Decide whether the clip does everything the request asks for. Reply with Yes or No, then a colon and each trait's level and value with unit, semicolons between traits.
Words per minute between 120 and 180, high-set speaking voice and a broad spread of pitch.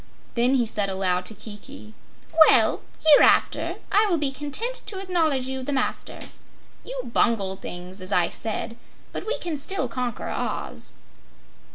Yes: average, 150 wpm; very high, 255 Hz; wide, 6.8 semitones